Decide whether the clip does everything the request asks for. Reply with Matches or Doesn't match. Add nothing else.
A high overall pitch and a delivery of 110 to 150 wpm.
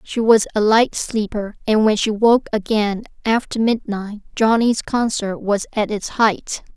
Doesn't match